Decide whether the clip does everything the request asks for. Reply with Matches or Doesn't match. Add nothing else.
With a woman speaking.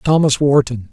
Doesn't match